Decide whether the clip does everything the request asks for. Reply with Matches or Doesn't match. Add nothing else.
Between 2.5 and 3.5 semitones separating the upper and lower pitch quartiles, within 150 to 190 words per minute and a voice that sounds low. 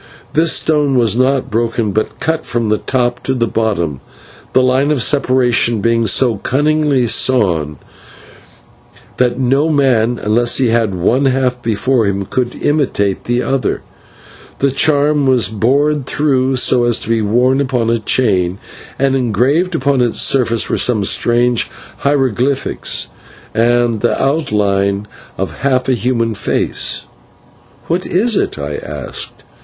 Doesn't match